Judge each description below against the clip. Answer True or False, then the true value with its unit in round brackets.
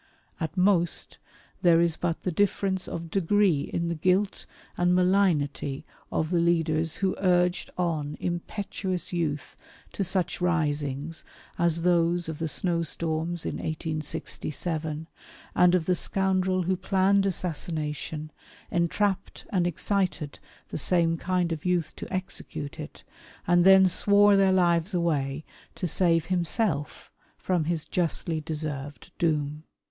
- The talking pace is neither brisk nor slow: False (130 wpm)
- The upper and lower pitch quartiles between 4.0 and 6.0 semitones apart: False (2.7 semitones)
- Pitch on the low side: False (170 Hz)